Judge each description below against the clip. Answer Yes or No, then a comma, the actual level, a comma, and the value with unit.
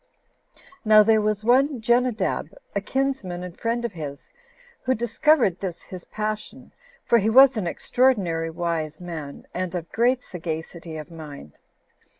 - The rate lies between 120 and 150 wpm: Yes, average, 145 wpm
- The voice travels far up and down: Yes, wide, 6.0 semitones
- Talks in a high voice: Yes, high, 200 Hz